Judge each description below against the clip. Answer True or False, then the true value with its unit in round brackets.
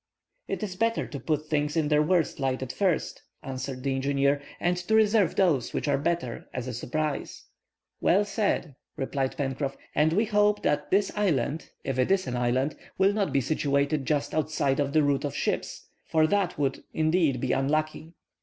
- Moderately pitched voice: True (150 Hz)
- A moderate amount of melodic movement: True (4.6 semitones)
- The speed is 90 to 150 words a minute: False (185 wpm)